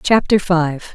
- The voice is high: No, medium, 175 Hz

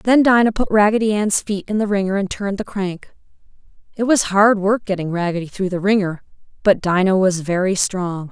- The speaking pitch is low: No, high, 195 Hz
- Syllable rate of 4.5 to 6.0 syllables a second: Yes, 5.4 syllables/s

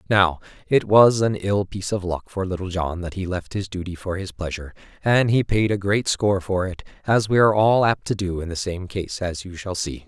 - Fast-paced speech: Yes, fast, 250 wpm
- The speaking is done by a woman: No, male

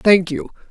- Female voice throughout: Yes, female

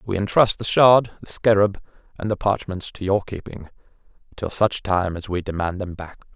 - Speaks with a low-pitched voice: Yes, low, 100 Hz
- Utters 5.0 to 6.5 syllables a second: Yes, 5.5 syllables/s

